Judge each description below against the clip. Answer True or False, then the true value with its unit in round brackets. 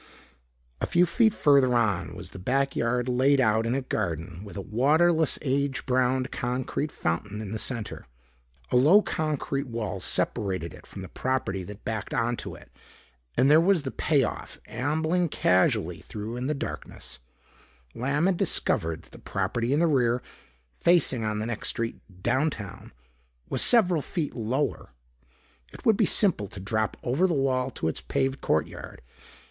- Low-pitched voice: True (125 Hz)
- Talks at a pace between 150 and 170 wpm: True (160 wpm)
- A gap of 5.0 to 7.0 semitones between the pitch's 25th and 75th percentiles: True (5.4 semitones)